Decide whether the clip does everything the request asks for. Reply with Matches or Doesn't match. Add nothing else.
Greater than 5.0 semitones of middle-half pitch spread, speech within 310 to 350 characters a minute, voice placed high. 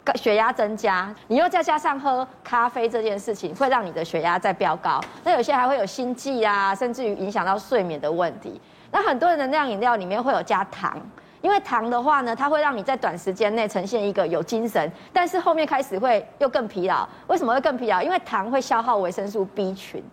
Matches